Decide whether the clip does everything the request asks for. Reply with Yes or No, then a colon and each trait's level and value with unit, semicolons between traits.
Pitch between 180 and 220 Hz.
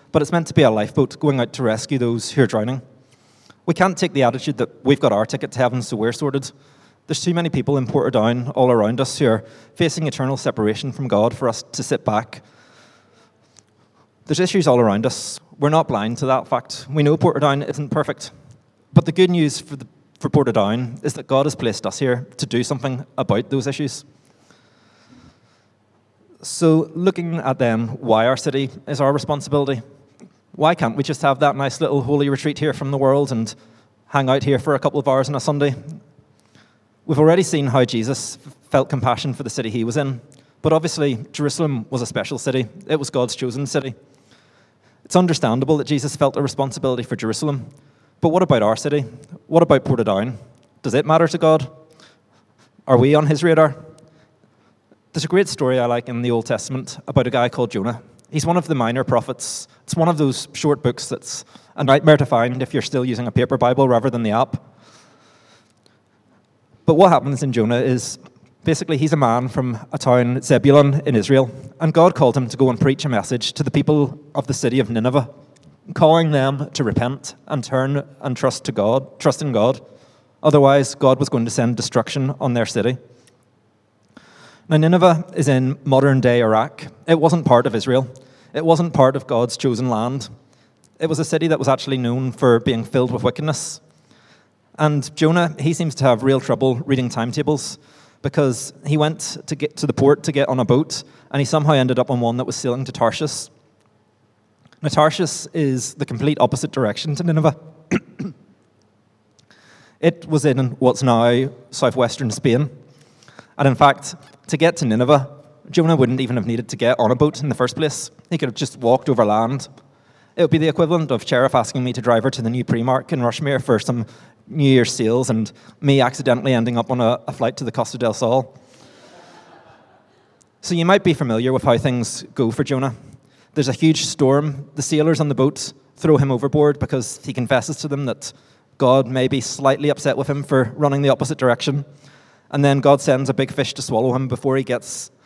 No: low, 135 Hz